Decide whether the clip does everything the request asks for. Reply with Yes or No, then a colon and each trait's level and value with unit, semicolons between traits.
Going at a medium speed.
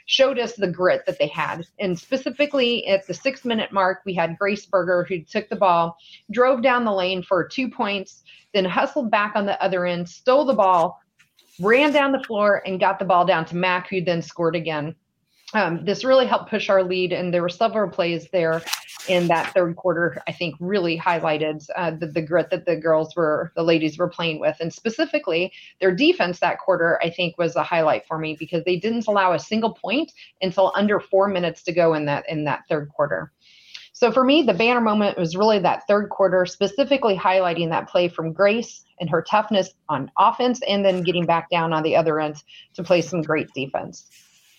No: fast, 210 wpm